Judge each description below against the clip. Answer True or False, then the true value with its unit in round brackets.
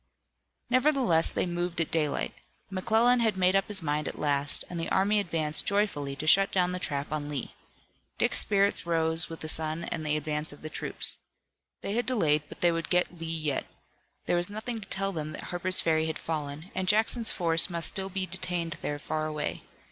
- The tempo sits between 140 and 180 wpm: False (200 wpm)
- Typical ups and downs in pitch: True (4.0 semitones)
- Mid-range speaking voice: True (170 Hz)